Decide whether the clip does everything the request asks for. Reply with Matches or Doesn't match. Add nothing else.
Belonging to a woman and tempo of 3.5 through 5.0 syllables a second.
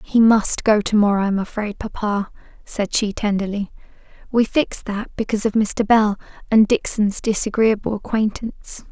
Matches